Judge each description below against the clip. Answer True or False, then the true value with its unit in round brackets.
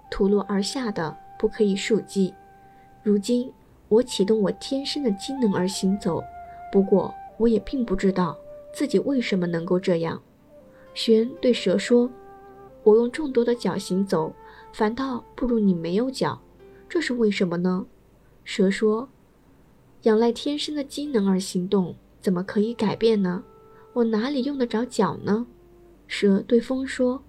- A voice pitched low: False (215 Hz)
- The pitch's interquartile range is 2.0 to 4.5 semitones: True (4.2 semitones)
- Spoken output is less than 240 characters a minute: True (215 characters per minute)